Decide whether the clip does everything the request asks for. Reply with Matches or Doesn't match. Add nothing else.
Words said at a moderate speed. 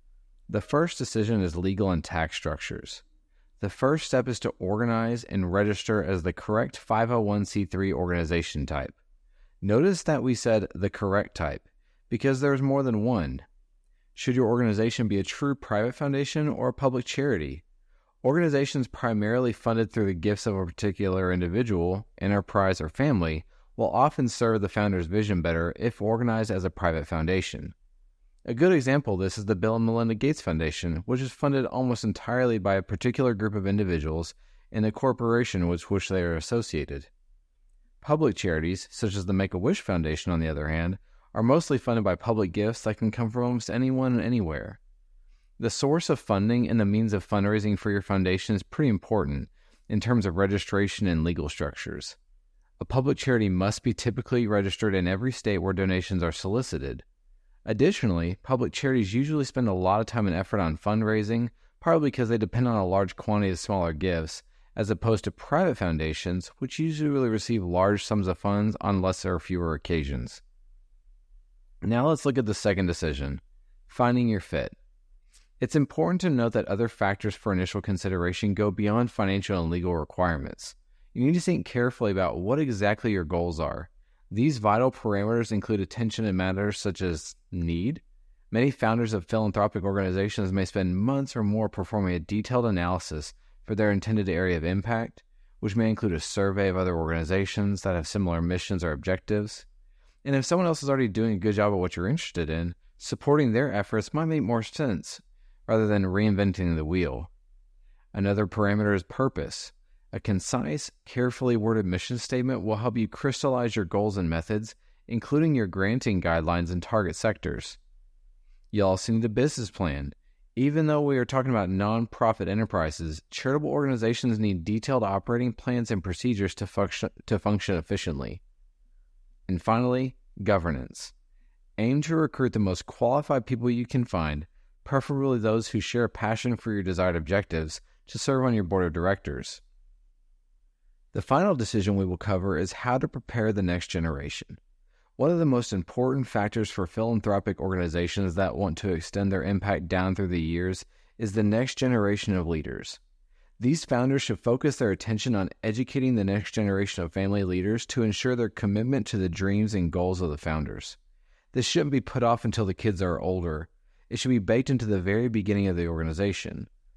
Matches